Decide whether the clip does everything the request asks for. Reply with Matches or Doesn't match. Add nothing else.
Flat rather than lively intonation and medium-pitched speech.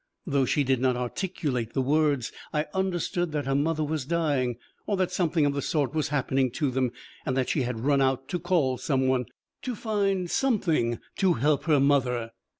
Doesn't match